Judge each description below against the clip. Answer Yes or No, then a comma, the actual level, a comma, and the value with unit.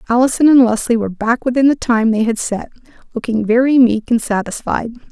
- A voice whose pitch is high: Yes, high, 235 Hz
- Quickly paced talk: No, average, 190 wpm